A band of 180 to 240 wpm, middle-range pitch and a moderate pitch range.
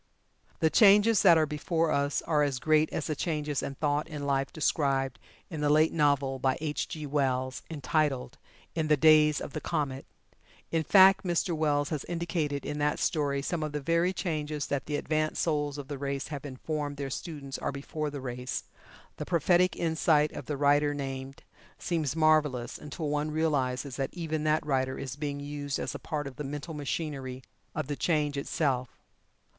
No: average, 185 wpm; medium, 150 Hz; narrow, 2.0 semitones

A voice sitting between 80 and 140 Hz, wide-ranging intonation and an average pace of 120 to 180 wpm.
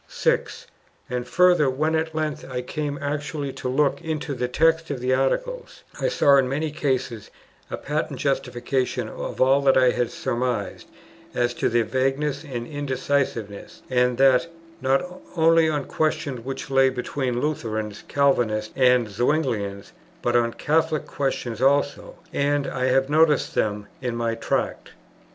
No: low, 135 Hz; average, 3.3 semitones; average, 150 wpm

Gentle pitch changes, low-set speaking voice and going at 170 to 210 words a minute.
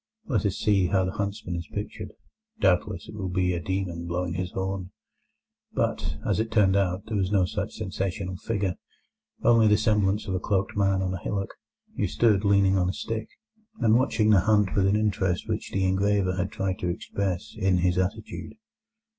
Yes: narrow, 2.1 semitones; very low, 95 Hz; average, 190 wpm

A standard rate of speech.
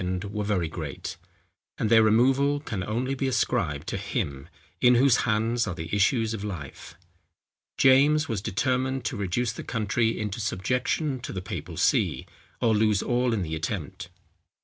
Yes: average, 160 wpm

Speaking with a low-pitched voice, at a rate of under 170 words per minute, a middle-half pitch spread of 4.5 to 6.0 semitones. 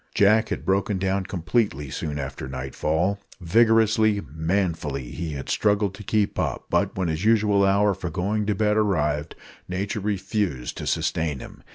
Yes: very low, 95 Hz; average, 160 wpm; average, 4.8 semitones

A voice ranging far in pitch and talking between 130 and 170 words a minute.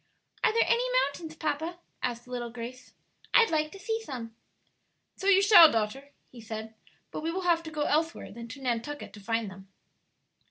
No: wide, 6.2 semitones; average, 185 wpm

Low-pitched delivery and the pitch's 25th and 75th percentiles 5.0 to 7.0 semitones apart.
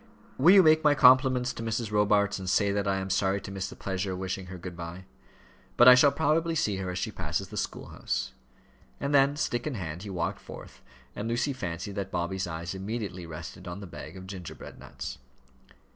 Yes: low, 100 Hz; average, 5.3 semitones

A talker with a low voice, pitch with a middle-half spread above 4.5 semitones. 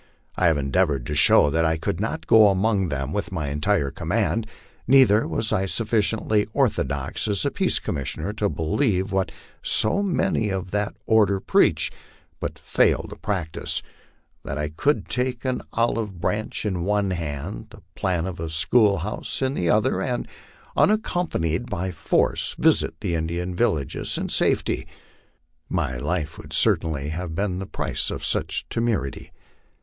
Yes: very low, 95 Hz; average, 5.2 semitones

